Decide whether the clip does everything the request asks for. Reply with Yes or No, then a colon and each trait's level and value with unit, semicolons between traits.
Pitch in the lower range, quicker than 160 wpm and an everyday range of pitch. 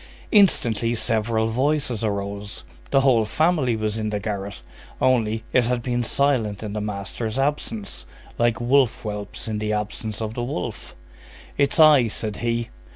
No: low, 115 Hz; average, 155 wpm; average, 3.0 semitones